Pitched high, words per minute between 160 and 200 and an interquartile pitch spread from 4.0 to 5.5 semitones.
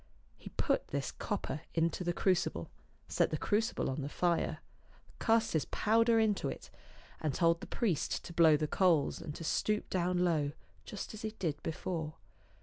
No: medium, 170 Hz; average, 170 wpm; average, 5.0 semitones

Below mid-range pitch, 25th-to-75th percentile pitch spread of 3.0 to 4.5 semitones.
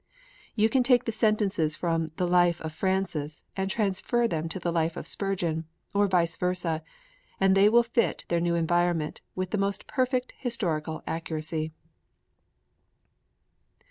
No: medium, 180 Hz; average, 3.9 semitones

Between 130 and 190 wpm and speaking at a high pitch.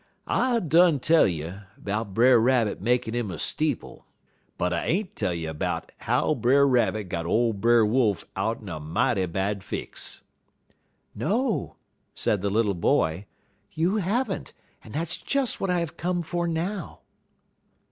No: average, 155 wpm; low, 120 Hz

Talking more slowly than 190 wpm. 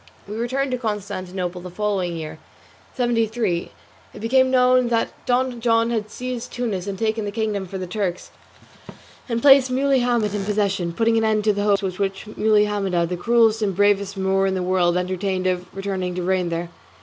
No: average, 195 wpm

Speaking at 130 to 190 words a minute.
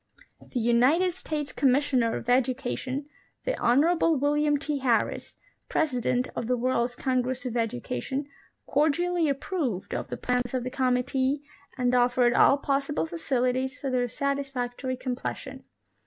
Yes: average, 140 wpm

